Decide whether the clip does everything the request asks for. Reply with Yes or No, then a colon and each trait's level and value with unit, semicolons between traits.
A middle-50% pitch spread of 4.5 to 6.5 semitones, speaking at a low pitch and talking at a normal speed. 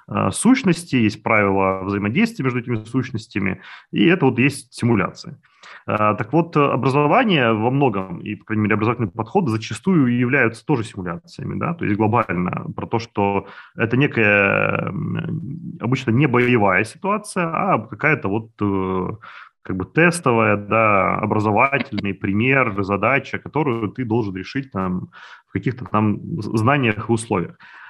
Yes: average, 5.2 semitones; low, 115 Hz; average, 130 wpm